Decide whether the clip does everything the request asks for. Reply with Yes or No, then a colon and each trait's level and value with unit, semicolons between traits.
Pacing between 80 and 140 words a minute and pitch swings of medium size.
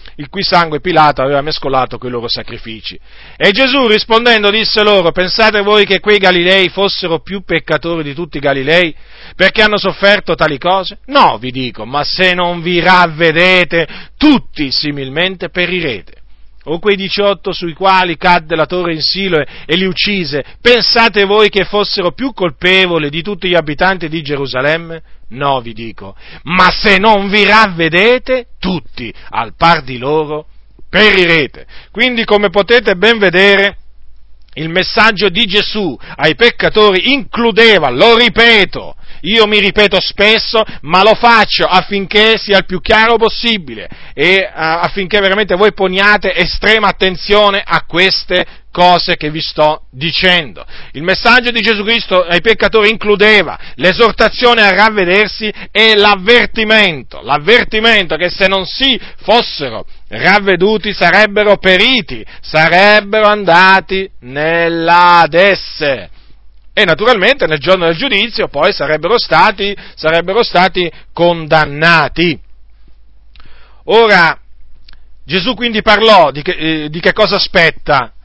Yes: average, 130 wpm; average, 4.6 semitones